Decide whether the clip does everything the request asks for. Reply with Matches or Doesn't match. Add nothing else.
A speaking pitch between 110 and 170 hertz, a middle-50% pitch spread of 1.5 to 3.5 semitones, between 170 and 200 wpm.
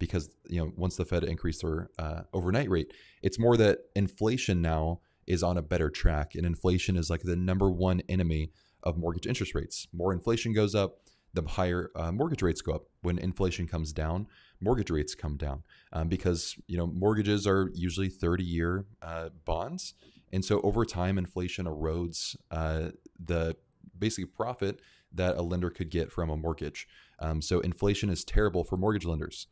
Doesn't match